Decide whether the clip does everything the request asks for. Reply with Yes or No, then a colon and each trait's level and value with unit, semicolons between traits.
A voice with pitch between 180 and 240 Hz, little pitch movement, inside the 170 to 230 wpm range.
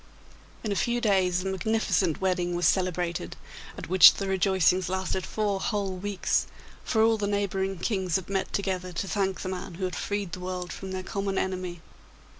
Yes: high, 190 Hz; narrow, 1.6 semitones; average, 185 wpm